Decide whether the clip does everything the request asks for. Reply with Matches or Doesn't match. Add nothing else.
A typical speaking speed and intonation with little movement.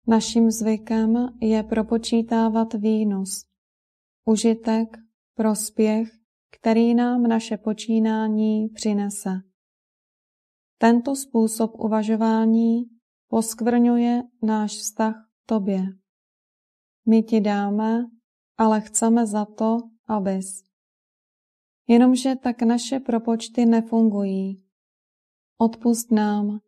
Doesn't match